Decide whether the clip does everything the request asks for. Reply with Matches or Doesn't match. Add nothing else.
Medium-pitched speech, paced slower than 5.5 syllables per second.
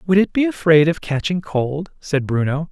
Matches